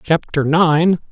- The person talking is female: No, male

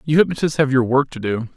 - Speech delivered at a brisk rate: Yes, fast, 270 wpm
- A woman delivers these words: No, male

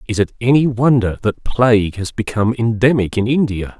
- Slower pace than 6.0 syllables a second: Yes, 5.4 syllables/s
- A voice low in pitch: Yes, low, 115 Hz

